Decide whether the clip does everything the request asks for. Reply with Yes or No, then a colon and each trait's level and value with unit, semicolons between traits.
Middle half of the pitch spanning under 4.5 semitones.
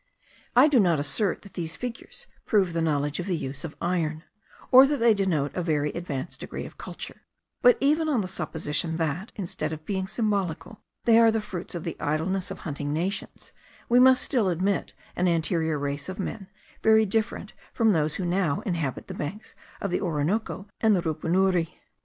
No: average, 5.1 semitones